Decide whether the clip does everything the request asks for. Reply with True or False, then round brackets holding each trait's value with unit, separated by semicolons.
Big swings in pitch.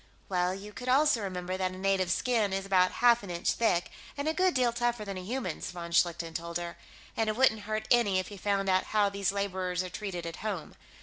False (3.4 semitones)